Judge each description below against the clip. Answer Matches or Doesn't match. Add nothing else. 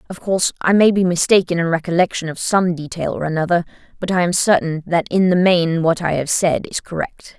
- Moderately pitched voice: Matches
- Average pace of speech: Doesn't match